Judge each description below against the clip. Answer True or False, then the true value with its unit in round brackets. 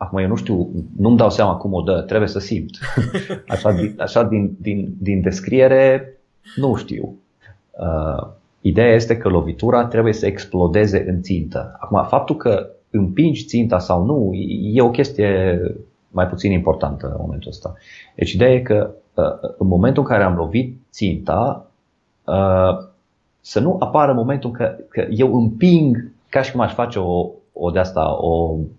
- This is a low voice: True (100 Hz)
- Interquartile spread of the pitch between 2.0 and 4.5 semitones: False (5.0 semitones)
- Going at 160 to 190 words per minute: True (165 wpm)